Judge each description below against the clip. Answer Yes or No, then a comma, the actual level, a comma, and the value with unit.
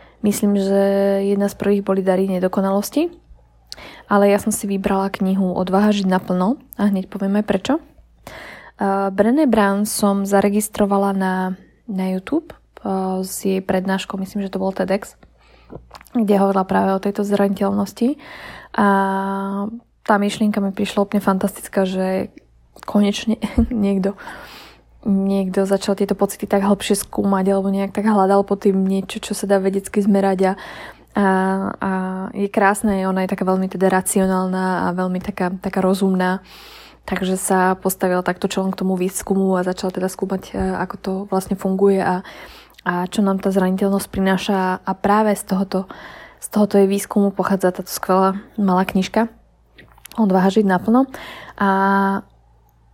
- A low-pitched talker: No, high, 195 Hz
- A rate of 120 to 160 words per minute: Yes, average, 145 wpm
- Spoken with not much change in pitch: Yes, narrow, 1.2 semitones